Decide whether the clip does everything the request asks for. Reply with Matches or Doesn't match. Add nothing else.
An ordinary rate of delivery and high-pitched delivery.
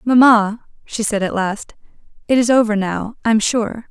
Matches